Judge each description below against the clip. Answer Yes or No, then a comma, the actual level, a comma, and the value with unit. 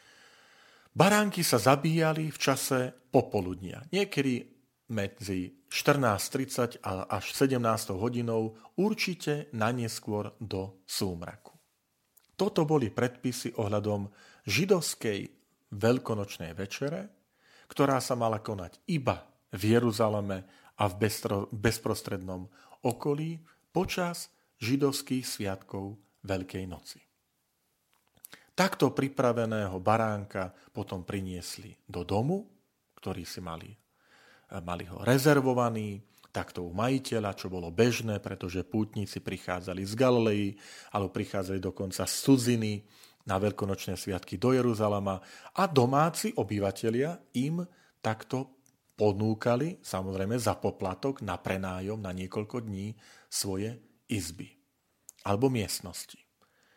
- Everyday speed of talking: No, slow, 95 wpm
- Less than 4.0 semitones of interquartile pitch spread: No, average, 5.0 semitones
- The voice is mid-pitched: No, low, 110 Hz